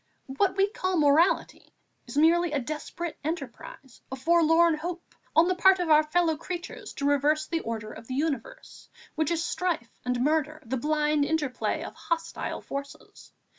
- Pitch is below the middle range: No, very high, 310 Hz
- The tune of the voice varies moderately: Yes, average, 3.3 semitones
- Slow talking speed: No, average, 165 wpm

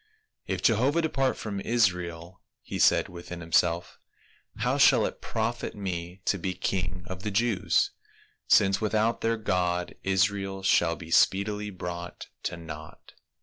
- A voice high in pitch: No, very low, 95 Hz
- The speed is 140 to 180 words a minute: Yes, average, 150 wpm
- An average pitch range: Yes, average, 3.4 semitones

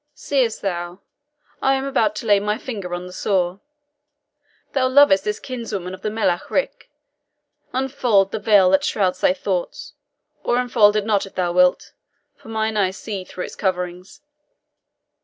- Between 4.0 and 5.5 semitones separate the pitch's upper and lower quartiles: No, average, 3.6 semitones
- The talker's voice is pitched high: Yes, high, 205 Hz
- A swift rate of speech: No, average, 160 wpm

